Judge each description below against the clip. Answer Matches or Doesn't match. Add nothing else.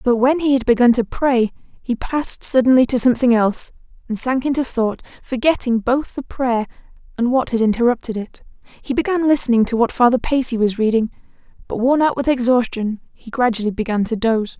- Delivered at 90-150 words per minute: Doesn't match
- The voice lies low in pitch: Doesn't match